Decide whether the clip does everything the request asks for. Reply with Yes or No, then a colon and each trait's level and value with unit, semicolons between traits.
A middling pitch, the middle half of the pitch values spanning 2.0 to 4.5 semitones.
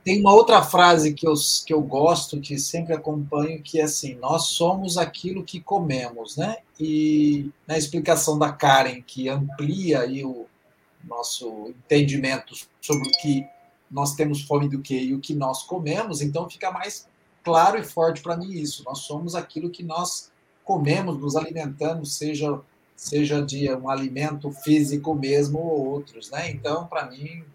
Yes: medium, 150 Hz; average, 2.8 semitones